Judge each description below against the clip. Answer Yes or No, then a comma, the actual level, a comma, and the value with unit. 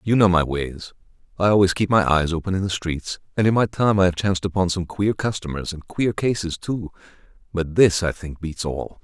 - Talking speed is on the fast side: Yes, fast, 225 wpm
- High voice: No, very low, 90 Hz